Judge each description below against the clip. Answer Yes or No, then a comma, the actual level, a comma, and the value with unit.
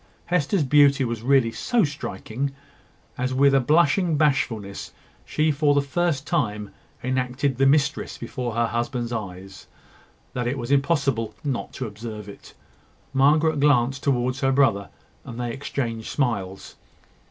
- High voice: No, low, 135 Hz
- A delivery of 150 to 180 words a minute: No, average, 140 wpm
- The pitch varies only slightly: No, average, 3.5 semitones